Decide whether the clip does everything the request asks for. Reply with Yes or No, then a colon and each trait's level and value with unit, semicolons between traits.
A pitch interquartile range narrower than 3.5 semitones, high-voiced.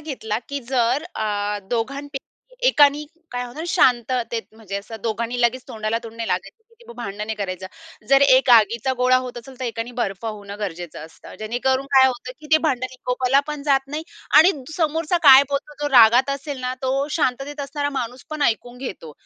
No: average, 3.8 semitones; very high, 250 Hz